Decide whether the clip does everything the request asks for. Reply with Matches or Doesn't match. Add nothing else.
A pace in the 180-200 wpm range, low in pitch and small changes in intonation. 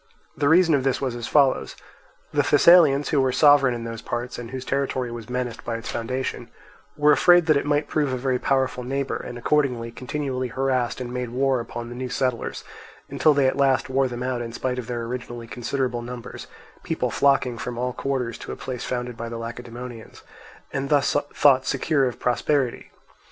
Matches